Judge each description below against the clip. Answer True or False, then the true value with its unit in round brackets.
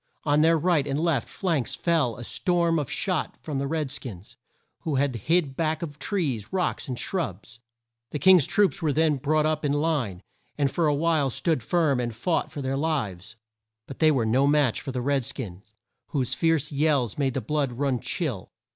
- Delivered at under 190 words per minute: False (195 wpm)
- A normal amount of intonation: True (4.0 semitones)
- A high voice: False (145 Hz)